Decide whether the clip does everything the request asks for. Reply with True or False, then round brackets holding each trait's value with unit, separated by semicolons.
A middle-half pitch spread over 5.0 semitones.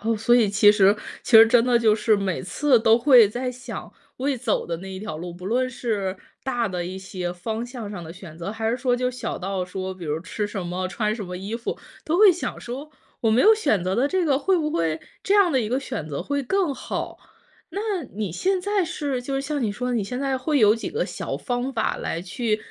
True (5.6 semitones)